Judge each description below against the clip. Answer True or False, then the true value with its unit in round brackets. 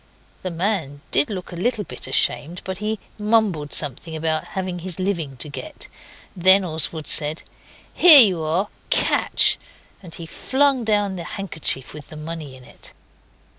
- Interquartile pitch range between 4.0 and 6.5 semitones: True (4.6 semitones)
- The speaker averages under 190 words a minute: True (160 wpm)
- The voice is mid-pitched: True (175 Hz)